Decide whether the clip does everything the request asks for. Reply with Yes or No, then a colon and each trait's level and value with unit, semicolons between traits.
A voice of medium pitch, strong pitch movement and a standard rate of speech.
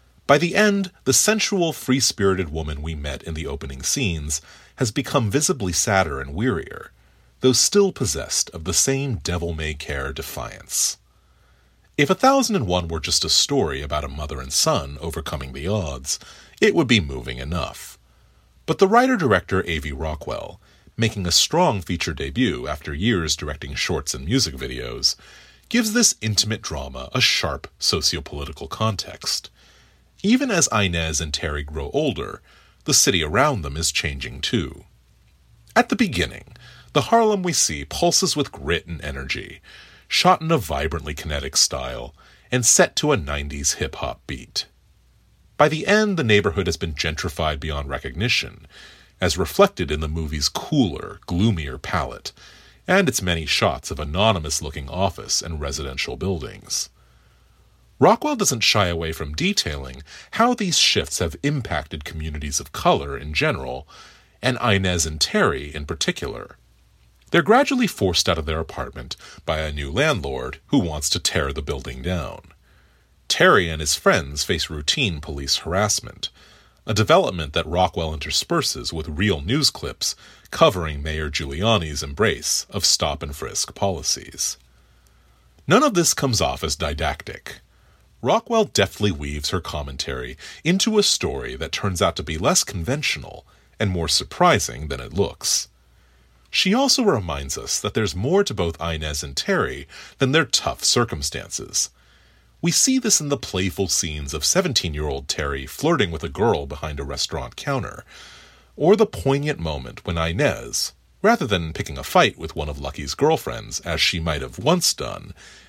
No: very low, 85 Hz; wide, 7.9 semitones; average, 155 wpm